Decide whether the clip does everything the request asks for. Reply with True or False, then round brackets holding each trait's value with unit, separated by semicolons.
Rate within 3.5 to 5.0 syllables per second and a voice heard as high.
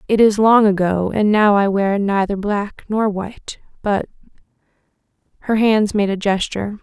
True (4.7 syllables/s; 205 Hz)